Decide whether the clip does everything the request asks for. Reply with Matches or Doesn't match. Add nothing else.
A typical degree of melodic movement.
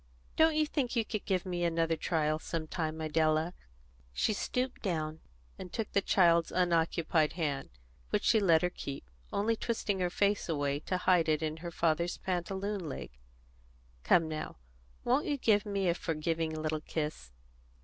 Matches